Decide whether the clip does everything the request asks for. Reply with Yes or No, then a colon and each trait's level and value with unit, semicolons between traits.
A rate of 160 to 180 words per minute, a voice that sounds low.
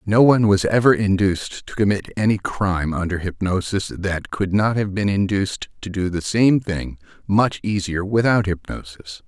Yes: average, 170 wpm; low, 100 Hz